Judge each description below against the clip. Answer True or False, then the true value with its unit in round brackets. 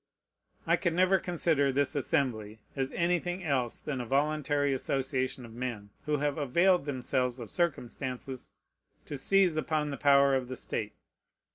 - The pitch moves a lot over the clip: False (3.4 semitones)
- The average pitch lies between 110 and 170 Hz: True (140 Hz)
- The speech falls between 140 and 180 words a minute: True (150 wpm)